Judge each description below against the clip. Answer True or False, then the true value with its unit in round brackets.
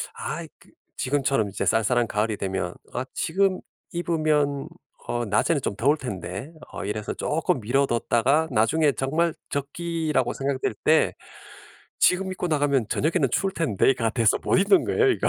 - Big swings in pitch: True (6.0 semitones)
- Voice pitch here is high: False (140 Hz)